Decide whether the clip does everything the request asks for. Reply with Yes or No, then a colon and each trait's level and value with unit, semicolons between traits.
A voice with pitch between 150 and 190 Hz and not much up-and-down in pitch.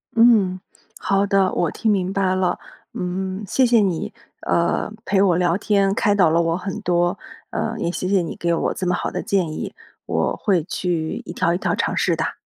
Yes: medium, 185 Hz; narrow, 2.3 semitones